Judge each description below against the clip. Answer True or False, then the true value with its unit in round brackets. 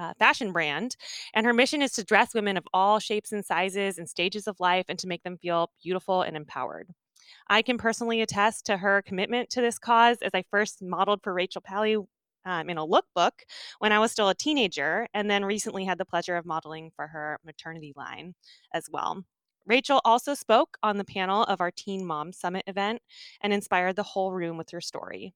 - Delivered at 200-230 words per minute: True (205 wpm)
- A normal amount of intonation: True (3.5 semitones)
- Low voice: False (200 Hz)